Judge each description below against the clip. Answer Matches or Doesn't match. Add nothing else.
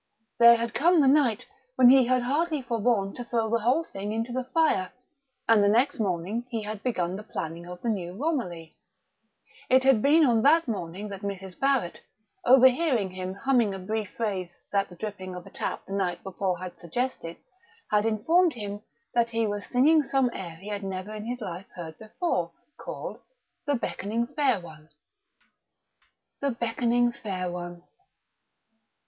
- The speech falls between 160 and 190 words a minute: Matches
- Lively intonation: Doesn't match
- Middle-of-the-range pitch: Doesn't match